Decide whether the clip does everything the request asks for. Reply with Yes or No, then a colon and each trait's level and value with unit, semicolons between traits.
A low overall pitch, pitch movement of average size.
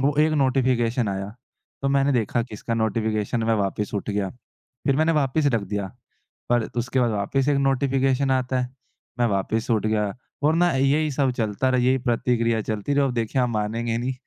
Yes: low, 120 Hz; average, 3.5 semitones